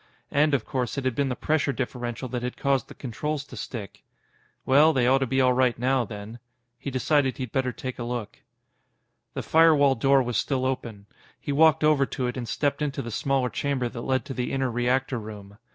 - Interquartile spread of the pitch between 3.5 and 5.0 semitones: No, narrow, 2.4 semitones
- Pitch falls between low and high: No, low, 130 Hz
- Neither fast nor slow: No, fast, 215 wpm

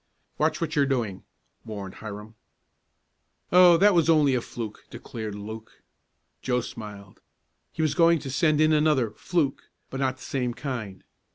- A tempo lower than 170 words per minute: Yes, average, 155 wpm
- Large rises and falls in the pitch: Yes, wide, 6.1 semitones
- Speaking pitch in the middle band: No, low, 130 Hz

